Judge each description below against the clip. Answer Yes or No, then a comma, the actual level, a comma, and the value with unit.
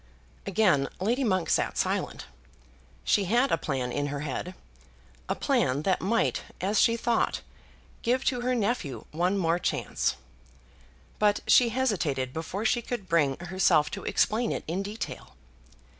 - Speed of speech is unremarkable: Yes, average, 145 wpm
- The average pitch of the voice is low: No, high, 190 Hz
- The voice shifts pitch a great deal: Yes, wide, 7.0 semitones